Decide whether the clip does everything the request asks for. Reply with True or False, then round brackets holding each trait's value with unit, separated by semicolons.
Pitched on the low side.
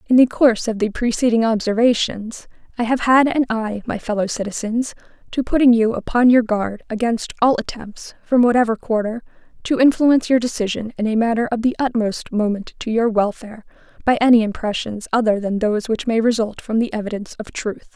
False (225 Hz)